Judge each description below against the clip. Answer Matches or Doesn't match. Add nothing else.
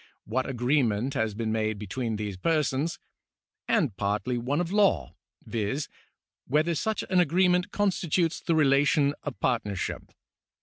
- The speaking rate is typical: Doesn't match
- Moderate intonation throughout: Doesn't match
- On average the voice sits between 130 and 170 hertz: Matches